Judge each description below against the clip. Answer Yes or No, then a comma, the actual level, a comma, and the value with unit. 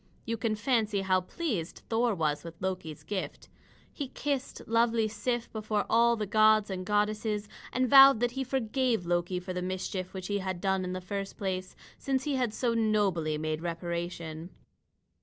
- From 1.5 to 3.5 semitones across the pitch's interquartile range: No, average, 4.1 semitones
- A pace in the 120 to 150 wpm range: No, average, 175 wpm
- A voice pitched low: No, high, 205 Hz